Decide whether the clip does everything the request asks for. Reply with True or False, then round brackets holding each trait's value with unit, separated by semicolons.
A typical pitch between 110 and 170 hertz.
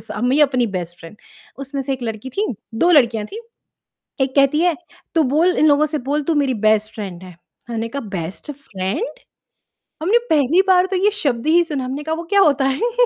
False (275 Hz)